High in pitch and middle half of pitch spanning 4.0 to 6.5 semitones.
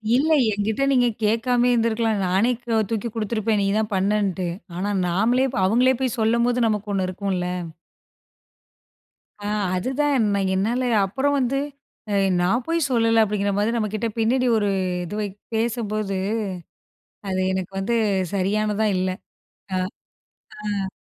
No: high, 220 Hz; average, 3.3 semitones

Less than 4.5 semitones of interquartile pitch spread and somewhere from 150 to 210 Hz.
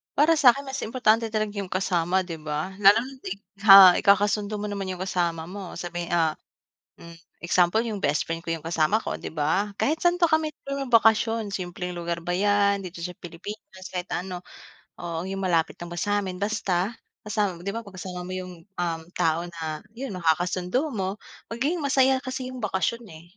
Yes: average, 4.0 semitones; high, 190 Hz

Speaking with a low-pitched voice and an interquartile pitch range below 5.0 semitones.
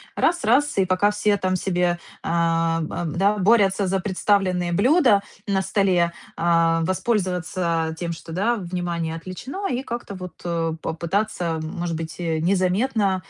No: medium, 185 Hz; average, 3.2 semitones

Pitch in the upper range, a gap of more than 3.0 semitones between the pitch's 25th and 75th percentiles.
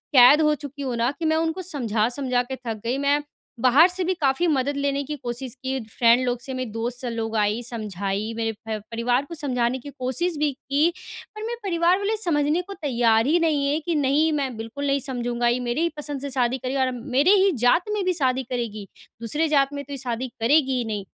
Yes: very high, 265 Hz; average, 3.9 semitones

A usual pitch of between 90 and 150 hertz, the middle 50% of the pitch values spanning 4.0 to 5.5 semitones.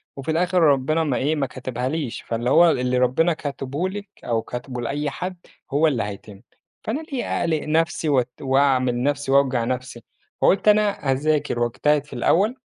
Yes: medium, 140 Hz; average, 4.3 semitones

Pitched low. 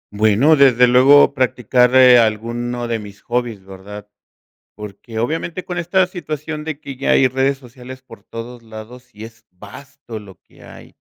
Yes: low, 125 Hz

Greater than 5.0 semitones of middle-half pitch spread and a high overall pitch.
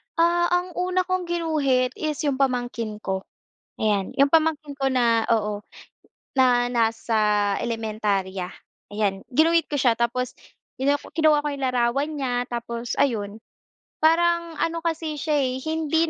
Yes: wide, 5.5 semitones; very high, 265 Hz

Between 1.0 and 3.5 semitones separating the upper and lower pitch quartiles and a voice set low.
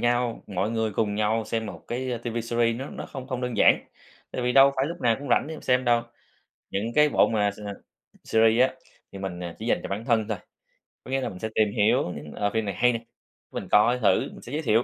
Yes: average, 2.9 semitones; low, 115 Hz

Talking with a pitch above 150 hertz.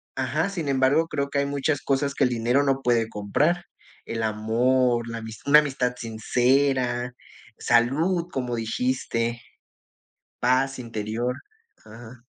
No: low, 125 Hz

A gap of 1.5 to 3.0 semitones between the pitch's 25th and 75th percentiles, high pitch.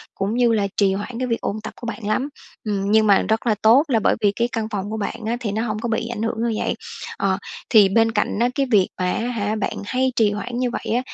Yes: narrow, 2.4 semitones; high, 220 Hz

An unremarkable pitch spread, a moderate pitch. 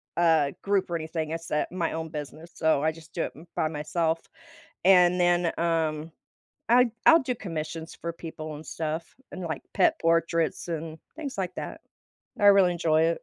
No: narrow, 1.8 semitones; medium, 165 Hz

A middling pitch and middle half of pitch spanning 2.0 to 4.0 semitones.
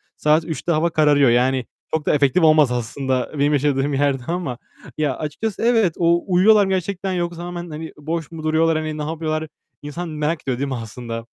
Yes: medium, 155 Hz; average, 3.4 semitones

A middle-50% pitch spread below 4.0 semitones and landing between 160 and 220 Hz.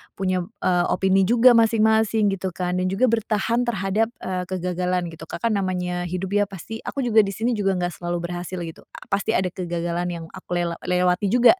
Yes: average, 3.5 semitones; medium, 185 Hz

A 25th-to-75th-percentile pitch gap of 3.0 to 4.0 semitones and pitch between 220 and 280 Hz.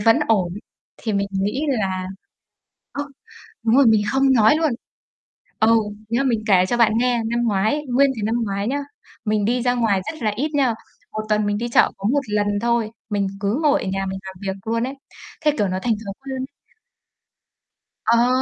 Yes: average, 3.5 semitones; high, 225 Hz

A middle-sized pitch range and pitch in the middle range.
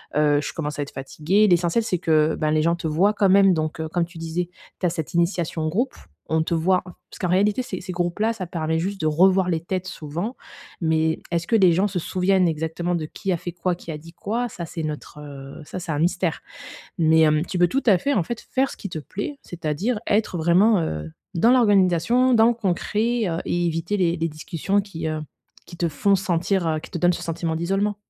Yes: average, 3.3 semitones; medium, 175 Hz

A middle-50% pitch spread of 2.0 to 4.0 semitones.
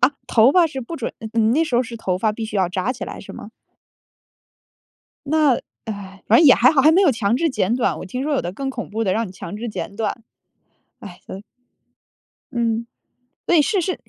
No: average, 4.7 semitones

